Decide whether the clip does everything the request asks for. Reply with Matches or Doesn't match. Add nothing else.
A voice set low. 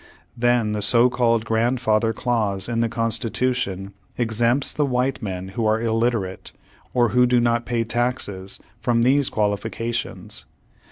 Matches